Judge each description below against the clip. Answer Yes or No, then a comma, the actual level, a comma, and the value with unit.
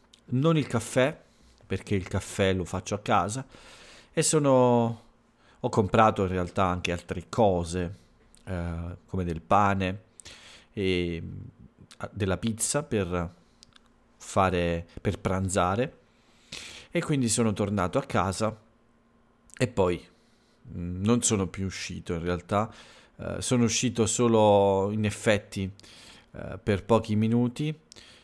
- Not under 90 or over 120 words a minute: Yes, slow, 115 wpm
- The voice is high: No, low, 105 Hz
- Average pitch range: Yes, average, 4.1 semitones